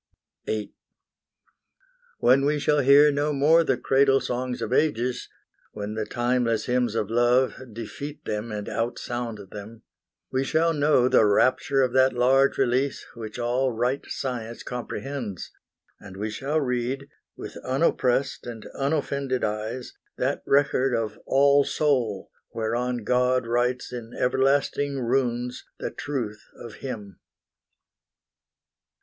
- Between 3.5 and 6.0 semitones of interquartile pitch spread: No, average, 2.9 semitones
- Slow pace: Yes, slow, 125 wpm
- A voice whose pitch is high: No, low, 125 Hz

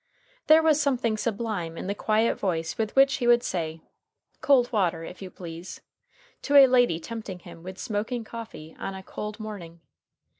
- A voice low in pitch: No, high, 215 Hz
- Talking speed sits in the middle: Yes, average, 175 wpm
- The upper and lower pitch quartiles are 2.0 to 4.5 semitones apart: No, average, 5.2 semitones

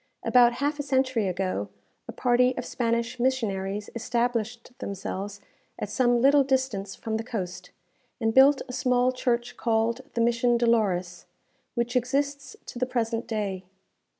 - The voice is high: Yes, high, 235 Hz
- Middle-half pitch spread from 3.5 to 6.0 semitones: No, average, 2.9 semitones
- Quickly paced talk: No, average, 145 wpm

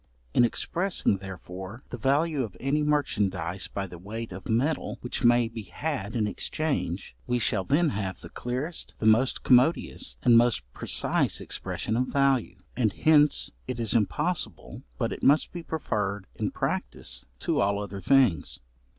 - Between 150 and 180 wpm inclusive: Yes, average, 160 wpm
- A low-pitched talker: Yes, low, 120 Hz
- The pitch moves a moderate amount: No, wide, 5.9 semitones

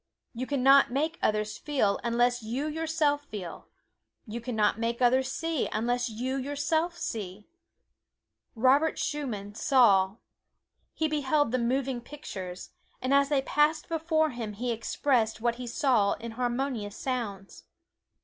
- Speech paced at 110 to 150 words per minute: Yes, average, 140 wpm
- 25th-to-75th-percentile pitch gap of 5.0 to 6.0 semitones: No, average, 4.3 semitones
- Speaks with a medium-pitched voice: No, very high, 250 Hz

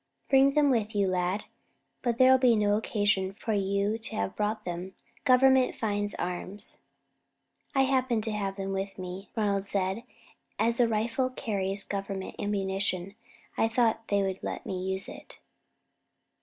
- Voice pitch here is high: Yes, high, 205 Hz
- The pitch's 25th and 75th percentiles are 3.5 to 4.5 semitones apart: No, average, 3.1 semitones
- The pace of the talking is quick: No, average, 155 wpm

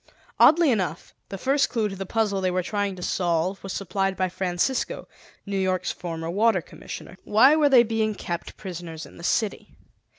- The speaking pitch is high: Yes, high, 195 Hz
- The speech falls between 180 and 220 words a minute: Yes, average, 185 wpm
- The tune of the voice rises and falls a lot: No, average, 3.5 semitones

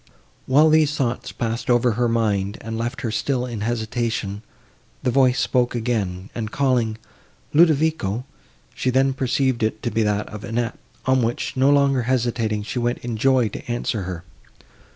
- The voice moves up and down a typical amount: Yes, average, 3.0 semitones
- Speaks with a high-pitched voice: No, low, 120 Hz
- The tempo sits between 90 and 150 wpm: No, average, 165 wpm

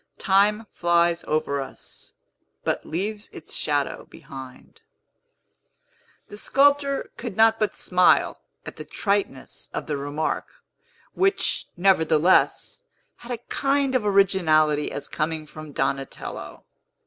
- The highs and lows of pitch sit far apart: Yes, wide, 6.3 semitones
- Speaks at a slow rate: Yes, slow, 115 wpm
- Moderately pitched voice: Yes, medium, 180 Hz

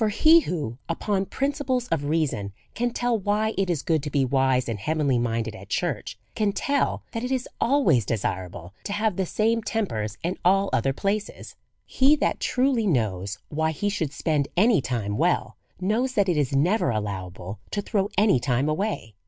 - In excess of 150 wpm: Yes, average, 185 wpm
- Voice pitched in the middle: Yes, medium, 170 Hz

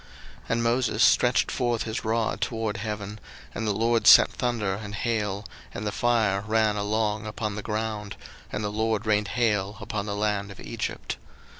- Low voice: Yes, low, 110 Hz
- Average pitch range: No, narrow, 1.4 semitones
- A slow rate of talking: No, average, 175 wpm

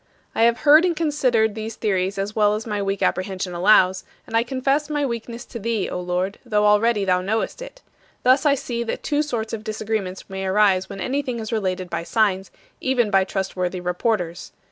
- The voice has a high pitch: Yes, high, 215 Hz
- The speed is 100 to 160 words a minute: No, average, 195 wpm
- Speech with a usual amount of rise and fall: Yes, average, 3.8 semitones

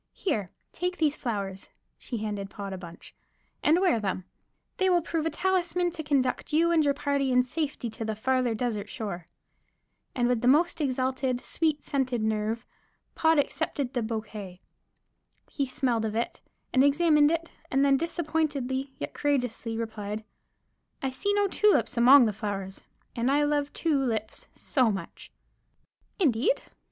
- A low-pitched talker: No, very high, 260 Hz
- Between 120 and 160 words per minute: Yes, average, 155 wpm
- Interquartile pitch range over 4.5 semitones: Yes, wide, 5.6 semitones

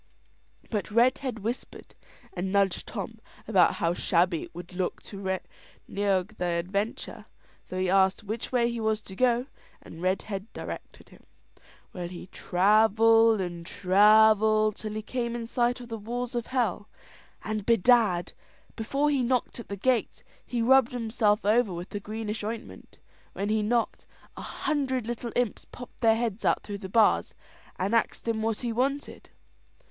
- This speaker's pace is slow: No, average, 160 wpm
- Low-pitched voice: No, high, 220 Hz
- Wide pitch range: No, average, 3.4 semitones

